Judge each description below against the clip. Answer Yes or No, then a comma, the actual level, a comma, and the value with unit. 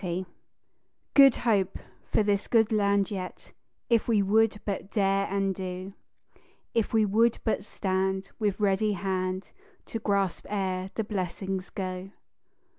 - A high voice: Yes, high, 195 Hz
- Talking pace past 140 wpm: No, slow, 135 wpm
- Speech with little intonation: Yes, narrow, 2.0 semitones